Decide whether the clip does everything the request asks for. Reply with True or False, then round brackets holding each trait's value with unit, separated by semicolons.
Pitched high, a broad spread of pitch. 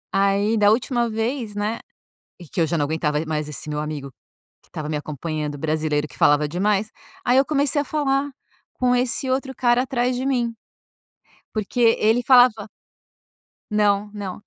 True (210 Hz; 7.9 semitones)